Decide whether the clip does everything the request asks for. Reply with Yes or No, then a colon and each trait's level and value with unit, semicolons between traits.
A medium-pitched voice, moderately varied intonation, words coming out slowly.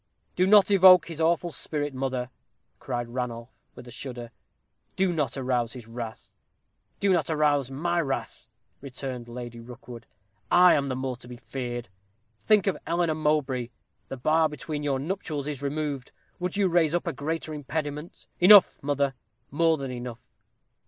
No: medium, 145 Hz; average, 4.7 semitones; average, 160 wpm